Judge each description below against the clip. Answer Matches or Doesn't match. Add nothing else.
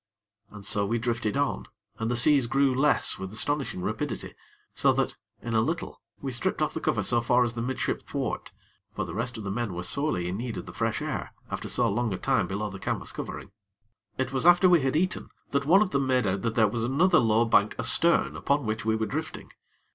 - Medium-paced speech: Doesn't match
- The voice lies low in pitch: Matches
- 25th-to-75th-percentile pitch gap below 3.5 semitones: Doesn't match